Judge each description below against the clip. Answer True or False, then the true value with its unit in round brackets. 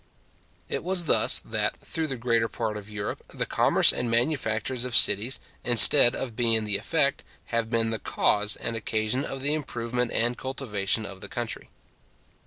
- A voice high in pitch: False (115 Hz)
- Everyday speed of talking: True (170 wpm)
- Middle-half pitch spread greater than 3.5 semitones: False (3.2 semitones)